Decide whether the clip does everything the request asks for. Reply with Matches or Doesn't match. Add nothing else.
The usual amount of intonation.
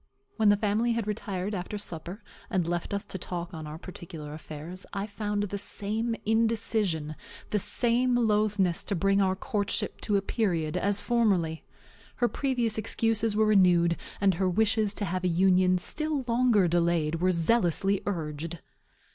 Matches